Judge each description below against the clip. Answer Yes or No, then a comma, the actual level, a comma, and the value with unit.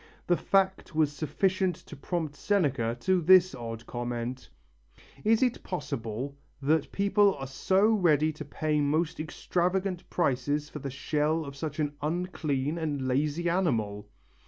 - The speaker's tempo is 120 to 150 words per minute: Yes, average, 140 wpm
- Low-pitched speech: No, medium, 155 Hz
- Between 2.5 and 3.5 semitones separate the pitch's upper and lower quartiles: No, average, 4.7 semitones